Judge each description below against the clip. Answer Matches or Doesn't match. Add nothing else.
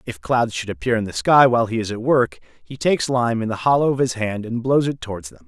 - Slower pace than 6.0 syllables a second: Doesn't match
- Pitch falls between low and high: Doesn't match